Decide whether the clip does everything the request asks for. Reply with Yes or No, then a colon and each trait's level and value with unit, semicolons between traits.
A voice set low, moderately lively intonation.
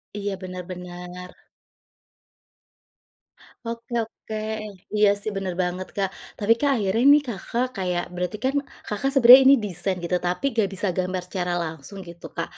No: high, 190 Hz; average, 3.6 semitones